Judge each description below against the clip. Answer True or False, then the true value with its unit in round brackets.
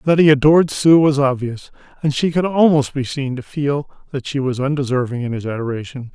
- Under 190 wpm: False (195 wpm)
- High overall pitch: False (140 Hz)